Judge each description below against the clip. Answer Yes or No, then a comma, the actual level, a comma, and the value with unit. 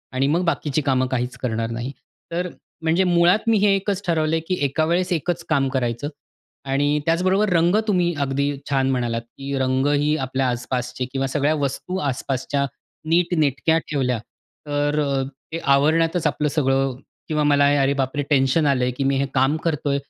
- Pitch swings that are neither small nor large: Yes, average, 3.6 semitones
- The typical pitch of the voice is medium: Yes, medium, 145 Hz